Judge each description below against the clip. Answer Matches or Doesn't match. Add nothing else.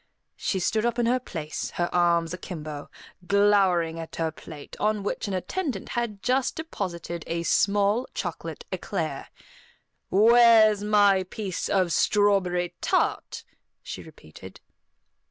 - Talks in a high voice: Matches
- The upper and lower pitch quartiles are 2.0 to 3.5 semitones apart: Doesn't match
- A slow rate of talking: Matches